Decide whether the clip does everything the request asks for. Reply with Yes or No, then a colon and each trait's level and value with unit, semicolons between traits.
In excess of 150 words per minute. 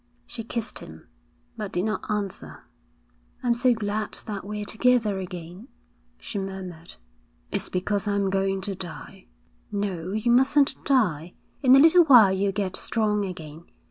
No: average, 145 wpm